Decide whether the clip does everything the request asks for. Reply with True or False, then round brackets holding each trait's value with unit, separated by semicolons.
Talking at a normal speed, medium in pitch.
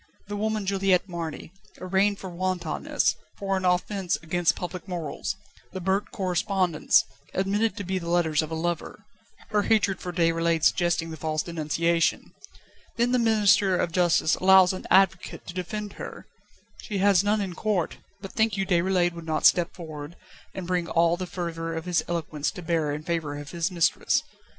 True (175 wpm; 180 Hz)